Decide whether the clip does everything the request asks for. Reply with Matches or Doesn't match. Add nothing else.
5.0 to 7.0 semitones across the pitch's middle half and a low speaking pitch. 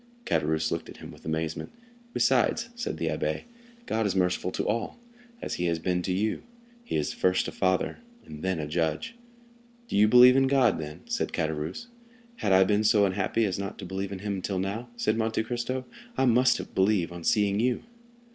Doesn't match